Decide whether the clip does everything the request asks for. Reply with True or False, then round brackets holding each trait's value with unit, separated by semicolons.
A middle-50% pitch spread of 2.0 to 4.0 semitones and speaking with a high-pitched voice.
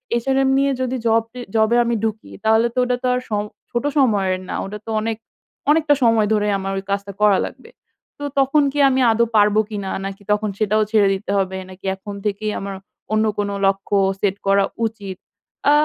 True (3.1 semitones; 215 Hz)